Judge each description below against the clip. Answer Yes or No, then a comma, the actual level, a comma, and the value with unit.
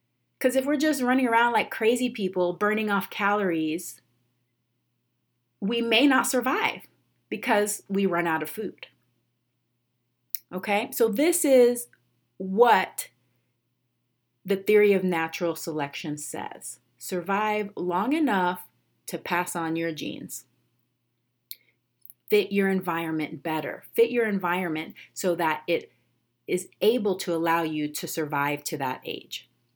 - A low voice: No, medium, 175 Hz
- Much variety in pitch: Yes, wide, 8.9 semitones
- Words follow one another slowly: Yes, slow, 125 wpm